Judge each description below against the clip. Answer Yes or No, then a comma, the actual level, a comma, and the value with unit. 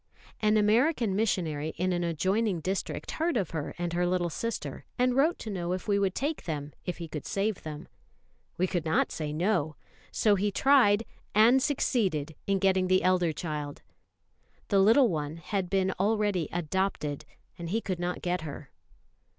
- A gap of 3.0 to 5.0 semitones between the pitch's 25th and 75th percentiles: Yes, average, 4.1 semitones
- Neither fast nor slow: Yes, average, 175 wpm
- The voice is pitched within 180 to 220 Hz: Yes, medium, 185 Hz